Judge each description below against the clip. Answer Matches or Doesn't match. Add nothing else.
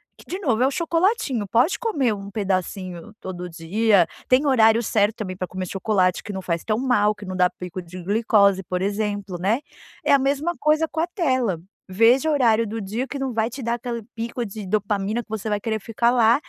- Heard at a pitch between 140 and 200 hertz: Doesn't match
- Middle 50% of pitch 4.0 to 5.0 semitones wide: Matches